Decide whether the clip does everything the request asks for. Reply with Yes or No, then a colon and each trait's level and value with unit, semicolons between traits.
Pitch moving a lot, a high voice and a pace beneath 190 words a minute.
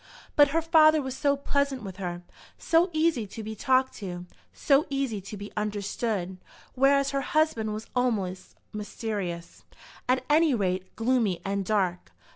Yes: wide, 6.1 semitones; high, 225 Hz; average, 150 wpm